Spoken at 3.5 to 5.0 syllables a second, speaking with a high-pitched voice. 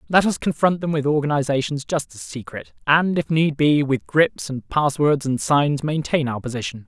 No: 4.9 syllables/s; medium, 145 Hz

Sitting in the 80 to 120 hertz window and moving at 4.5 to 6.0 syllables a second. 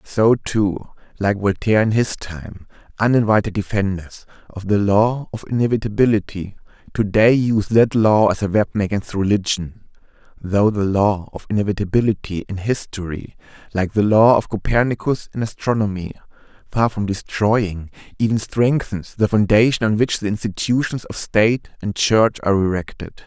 Yes: low, 105 Hz; 5.0 syllables/s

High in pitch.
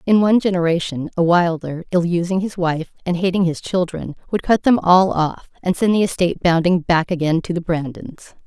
No: medium, 175 Hz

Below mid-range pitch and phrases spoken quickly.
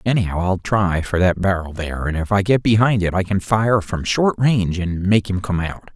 Yes: very low, 95 Hz; fast, 240 wpm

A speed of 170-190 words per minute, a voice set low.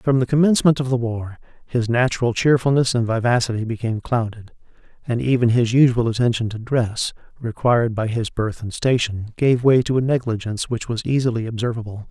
Yes: average, 175 wpm; low, 120 Hz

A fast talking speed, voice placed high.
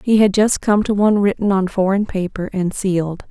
Yes: fast, 220 wpm; high, 195 Hz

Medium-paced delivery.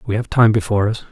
No: fast, 270 wpm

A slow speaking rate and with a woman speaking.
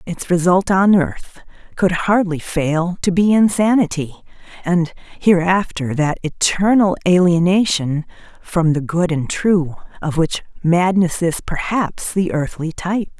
Yes: slow, 125 wpm; female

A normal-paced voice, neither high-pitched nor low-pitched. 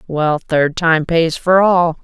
Yes: average, 175 wpm; medium, 165 Hz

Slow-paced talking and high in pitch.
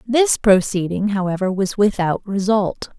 Yes: slow, 120 wpm; high, 200 Hz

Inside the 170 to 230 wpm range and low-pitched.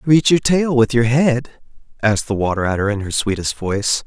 Yes: fast, 205 wpm; low, 120 Hz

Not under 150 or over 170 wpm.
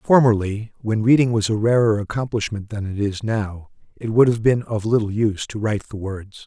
No: fast, 205 wpm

